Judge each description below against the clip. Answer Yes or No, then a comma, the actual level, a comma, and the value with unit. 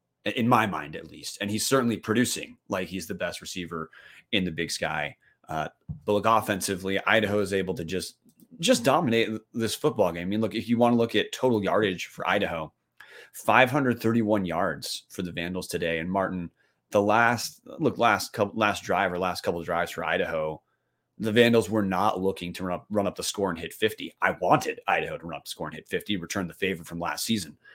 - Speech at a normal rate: No, fast, 215 wpm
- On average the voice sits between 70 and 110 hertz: Yes, low, 100 Hz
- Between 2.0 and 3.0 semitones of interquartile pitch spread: No, average, 3.7 semitones